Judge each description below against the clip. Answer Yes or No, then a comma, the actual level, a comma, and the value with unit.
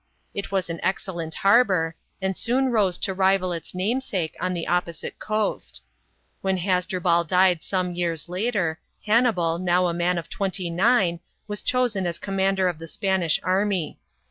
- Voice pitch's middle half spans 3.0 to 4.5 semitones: No, narrow, 2.4 semitones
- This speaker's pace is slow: No, average, 160 wpm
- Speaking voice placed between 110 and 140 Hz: No, medium, 185 Hz